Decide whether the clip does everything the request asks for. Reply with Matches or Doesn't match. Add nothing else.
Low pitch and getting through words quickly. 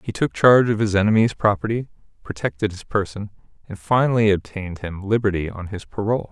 Doesn't match